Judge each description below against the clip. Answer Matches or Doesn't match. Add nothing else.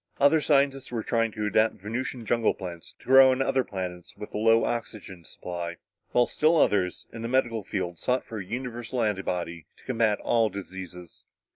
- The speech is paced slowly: Doesn't match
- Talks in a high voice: Doesn't match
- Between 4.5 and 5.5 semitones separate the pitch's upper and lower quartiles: Matches